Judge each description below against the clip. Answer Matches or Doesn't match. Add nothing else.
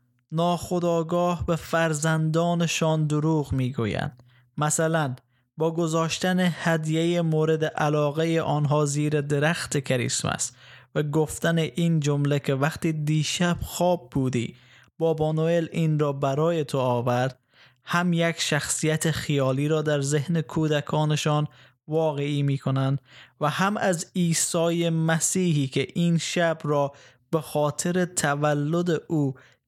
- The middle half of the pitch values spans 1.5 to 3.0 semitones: Matches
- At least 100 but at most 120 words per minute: Matches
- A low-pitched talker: Doesn't match